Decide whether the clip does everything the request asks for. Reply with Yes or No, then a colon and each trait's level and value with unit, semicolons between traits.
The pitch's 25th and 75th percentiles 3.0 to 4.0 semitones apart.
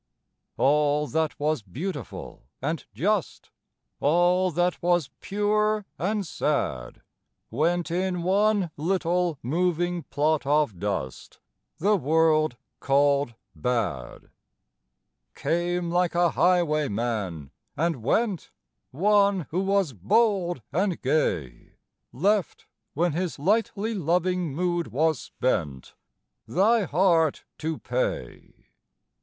No: average, 4.6 semitones